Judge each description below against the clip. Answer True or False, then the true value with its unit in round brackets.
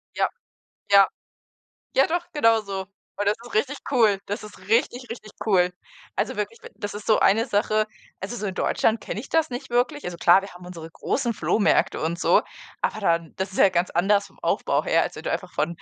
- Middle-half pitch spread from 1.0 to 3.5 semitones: False (3.9 semitones)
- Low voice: False (205 Hz)